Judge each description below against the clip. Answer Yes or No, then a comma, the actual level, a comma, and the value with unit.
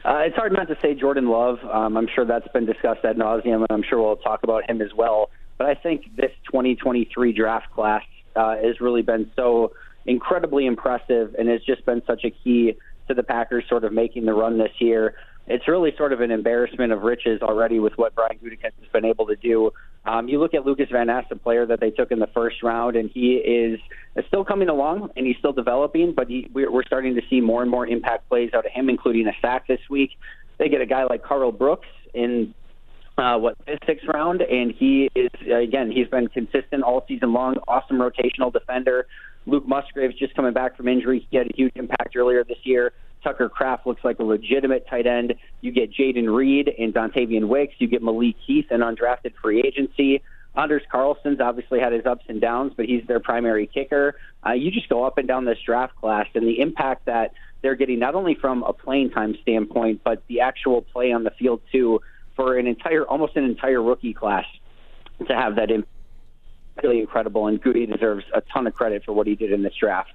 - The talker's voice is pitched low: Yes, low, 120 Hz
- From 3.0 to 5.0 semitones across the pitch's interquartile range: No, narrow, 2.4 semitones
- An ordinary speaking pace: No, fast, 220 wpm